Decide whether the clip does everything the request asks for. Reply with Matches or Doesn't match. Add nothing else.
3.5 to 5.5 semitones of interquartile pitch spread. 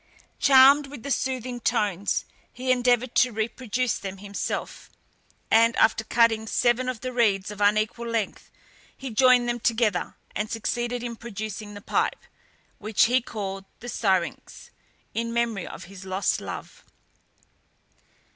Doesn't match